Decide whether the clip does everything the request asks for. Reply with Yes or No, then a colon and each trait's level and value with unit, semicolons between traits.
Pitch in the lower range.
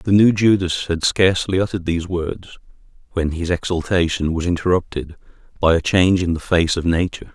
Yes: very low, 90 Hz